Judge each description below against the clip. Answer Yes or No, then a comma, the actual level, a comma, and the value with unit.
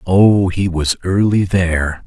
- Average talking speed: Yes, average, 145 wpm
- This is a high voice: No, very low, 90 Hz